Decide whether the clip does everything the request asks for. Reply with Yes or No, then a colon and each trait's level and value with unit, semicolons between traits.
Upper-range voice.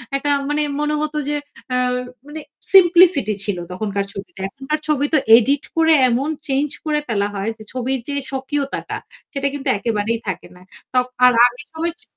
Yes: very high, 270 Hz